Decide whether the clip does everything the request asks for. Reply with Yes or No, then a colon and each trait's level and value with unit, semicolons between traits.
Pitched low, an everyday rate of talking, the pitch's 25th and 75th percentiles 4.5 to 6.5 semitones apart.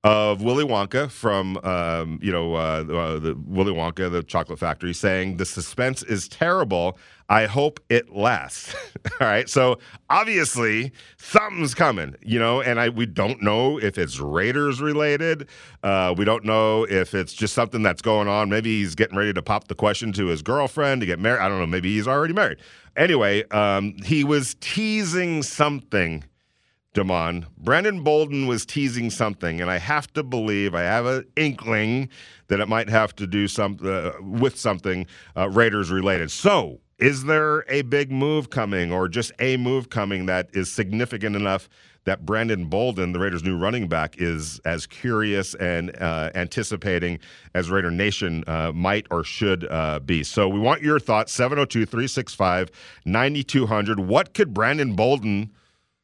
Yes: low, 105 Hz; average, 170 wpm; average, 5.3 semitones